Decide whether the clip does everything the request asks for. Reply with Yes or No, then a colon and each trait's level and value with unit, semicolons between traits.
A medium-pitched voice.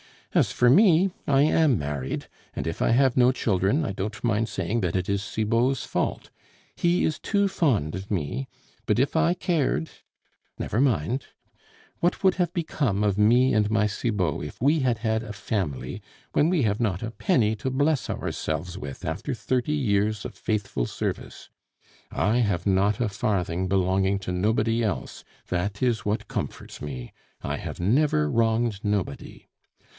No: low, 110 Hz